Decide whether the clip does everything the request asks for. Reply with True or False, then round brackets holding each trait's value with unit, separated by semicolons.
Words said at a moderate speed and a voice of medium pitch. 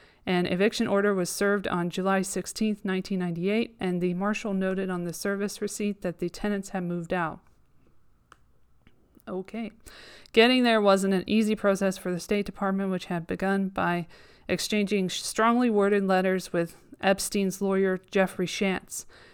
False (145 wpm; 195 Hz)